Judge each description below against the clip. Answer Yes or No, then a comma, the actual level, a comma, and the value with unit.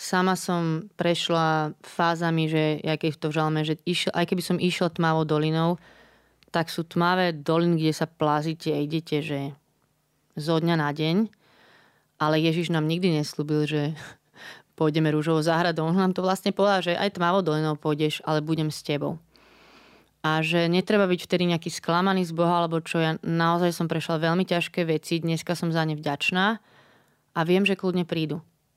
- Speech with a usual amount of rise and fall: No, narrow, 2.1 semitones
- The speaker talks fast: Yes, fast, 170 wpm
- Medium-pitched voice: Yes, medium, 165 Hz